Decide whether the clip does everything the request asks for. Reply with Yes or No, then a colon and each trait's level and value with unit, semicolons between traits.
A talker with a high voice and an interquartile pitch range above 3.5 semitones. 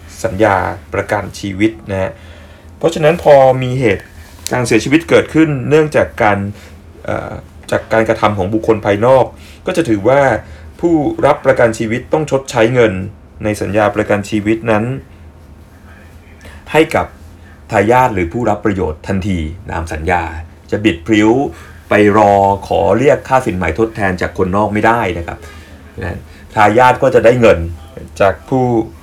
No: low, 100 Hz; average, 4.6 semitones